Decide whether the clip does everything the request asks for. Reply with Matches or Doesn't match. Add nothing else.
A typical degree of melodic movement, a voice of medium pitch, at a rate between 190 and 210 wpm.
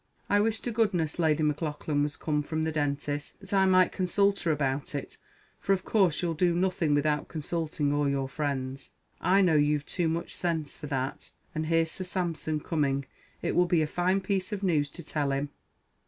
Matches